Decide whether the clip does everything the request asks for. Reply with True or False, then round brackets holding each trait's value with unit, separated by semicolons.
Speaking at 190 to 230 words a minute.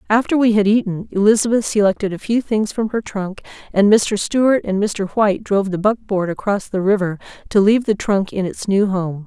True (205 wpm)